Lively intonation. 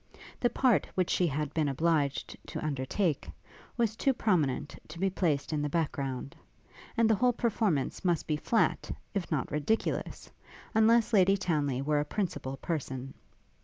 Yes: wide, 6.5 semitones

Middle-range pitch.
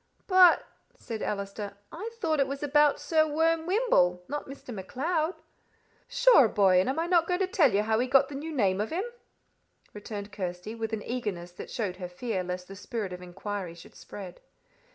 No: high, 225 Hz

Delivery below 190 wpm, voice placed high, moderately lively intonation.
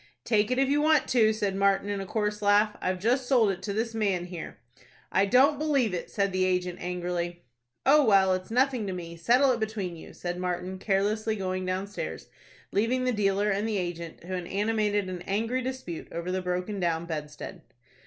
No: average, 200 wpm; high, 200 Hz; average, 3.6 semitones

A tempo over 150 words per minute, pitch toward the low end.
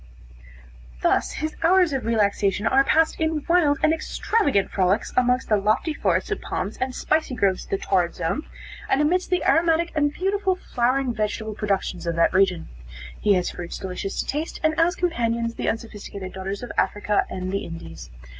No: average, 175 wpm; high, 235 Hz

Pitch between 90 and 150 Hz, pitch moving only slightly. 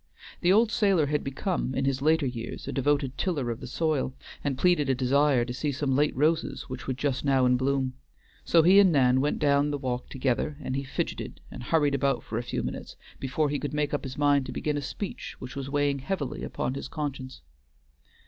Yes: medium, 140 Hz; narrow, 2.3 semitones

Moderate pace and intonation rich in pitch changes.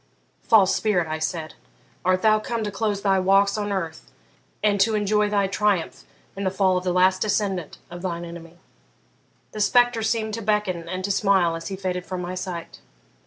No: average, 190 wpm; narrow, 2.6 semitones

